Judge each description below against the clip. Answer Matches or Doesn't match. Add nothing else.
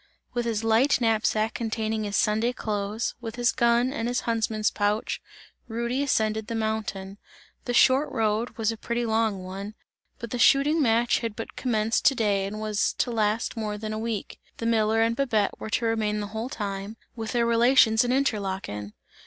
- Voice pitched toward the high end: Matches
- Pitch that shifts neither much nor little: Doesn't match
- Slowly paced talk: Doesn't match